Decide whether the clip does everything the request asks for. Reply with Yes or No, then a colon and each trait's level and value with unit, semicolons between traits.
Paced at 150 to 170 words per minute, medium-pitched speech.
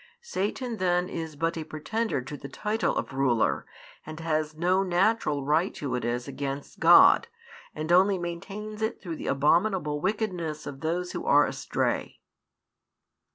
Yes: average, 155 wpm; medium, 165 Hz